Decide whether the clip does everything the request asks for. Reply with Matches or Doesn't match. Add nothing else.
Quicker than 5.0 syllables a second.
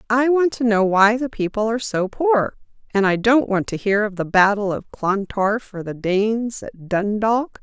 Doesn't match